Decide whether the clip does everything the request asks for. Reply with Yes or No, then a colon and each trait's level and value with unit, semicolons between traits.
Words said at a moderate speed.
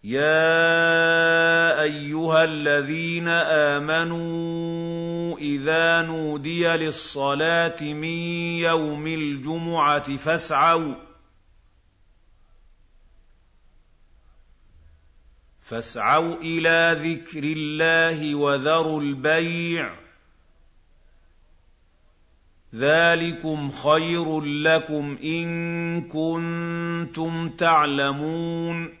No: slow, 50 wpm